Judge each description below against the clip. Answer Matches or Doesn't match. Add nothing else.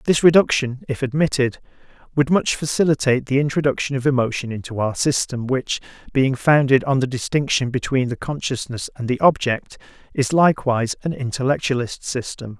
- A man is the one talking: Matches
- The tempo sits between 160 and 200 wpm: Doesn't match